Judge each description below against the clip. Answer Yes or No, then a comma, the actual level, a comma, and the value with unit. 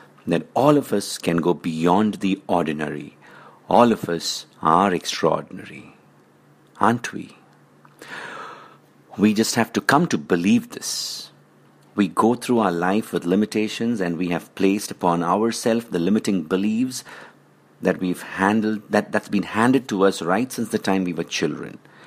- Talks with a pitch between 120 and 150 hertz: No, low, 100 Hz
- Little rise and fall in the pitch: No, average, 3.9 semitones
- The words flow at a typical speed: Yes, average, 150 wpm